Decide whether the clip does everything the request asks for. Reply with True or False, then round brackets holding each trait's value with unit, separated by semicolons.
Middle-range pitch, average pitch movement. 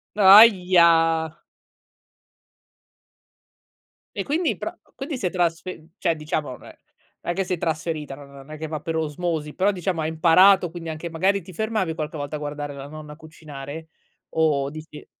True (160 Hz; 3.1 semitones)